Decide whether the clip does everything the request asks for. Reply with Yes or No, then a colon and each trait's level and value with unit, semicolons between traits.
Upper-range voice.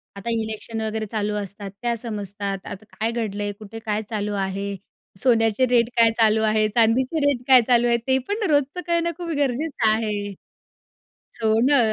Yes: high, 225 Hz